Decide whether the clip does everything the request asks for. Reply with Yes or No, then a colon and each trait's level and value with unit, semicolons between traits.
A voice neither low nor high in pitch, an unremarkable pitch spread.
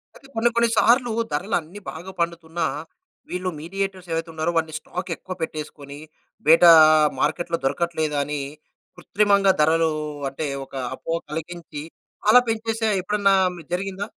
Yes: medium, 170 Hz; average, 3.7 semitones